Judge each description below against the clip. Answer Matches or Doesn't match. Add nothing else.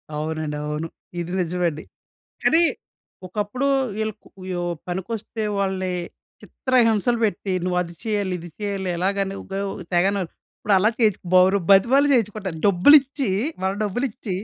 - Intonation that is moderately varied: Matches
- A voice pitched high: Matches